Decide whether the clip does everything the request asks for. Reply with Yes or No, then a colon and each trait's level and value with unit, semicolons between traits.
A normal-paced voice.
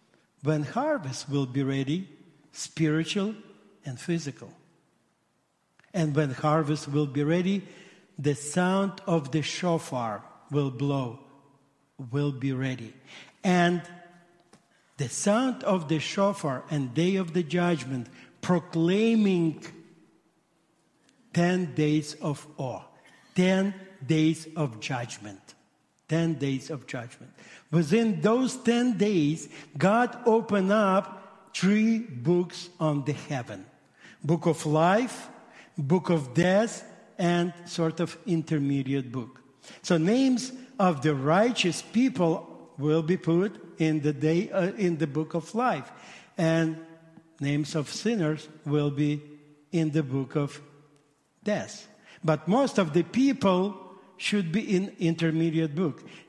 No: slow, 115 wpm